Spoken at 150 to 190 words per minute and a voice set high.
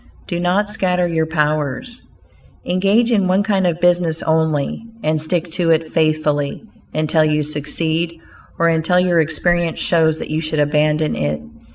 No: average, 155 wpm; medium, 160 Hz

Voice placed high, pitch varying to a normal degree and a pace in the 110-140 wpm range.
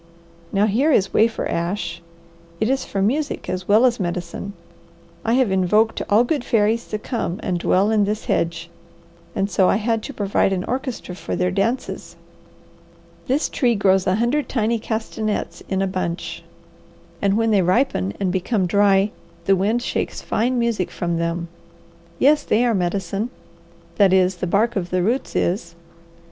No: high, 205 Hz; average, 3.9 semitones; average, 165 wpm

